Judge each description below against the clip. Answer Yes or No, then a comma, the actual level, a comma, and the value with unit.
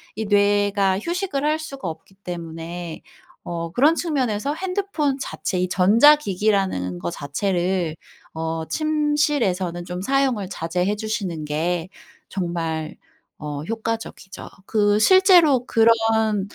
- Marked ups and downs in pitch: Yes, wide, 7.6 semitones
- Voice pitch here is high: Yes, high, 205 Hz